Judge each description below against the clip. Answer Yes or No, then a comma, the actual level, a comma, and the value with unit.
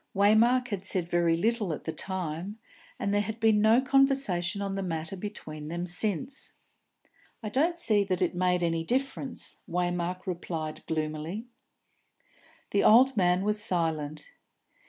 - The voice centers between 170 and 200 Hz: Yes, high, 190 Hz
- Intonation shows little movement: No, average, 4.2 semitones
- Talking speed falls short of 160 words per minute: Yes, average, 145 wpm